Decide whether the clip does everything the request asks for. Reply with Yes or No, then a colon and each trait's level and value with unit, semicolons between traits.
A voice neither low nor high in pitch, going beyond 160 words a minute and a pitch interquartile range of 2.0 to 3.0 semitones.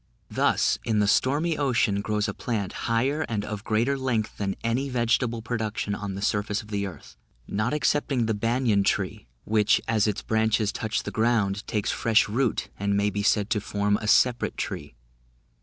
No: low, 110 Hz; average, 180 wpm; narrow, 2.5 semitones